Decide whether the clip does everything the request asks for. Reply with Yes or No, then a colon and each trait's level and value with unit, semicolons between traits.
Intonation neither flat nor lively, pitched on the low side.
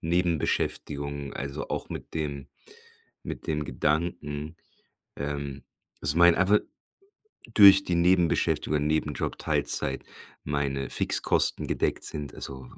Yes: average, 3.2 semitones; very low, 75 Hz